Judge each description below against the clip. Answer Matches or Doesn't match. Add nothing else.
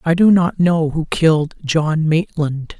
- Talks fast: Doesn't match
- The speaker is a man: Matches